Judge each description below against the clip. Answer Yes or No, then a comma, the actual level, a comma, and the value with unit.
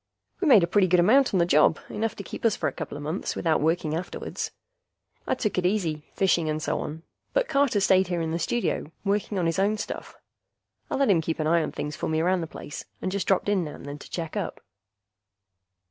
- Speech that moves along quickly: Yes, fast, 240 wpm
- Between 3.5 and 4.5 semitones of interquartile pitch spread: Yes, average, 4.1 semitones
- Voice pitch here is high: No, medium, 175 Hz